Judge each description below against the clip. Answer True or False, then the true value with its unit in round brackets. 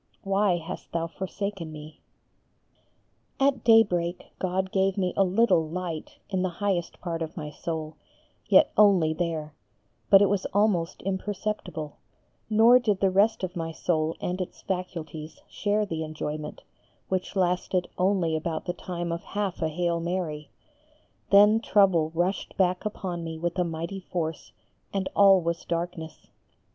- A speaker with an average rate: True (150 wpm)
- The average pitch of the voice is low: False (180 Hz)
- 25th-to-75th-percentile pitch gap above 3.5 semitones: False (3.1 semitones)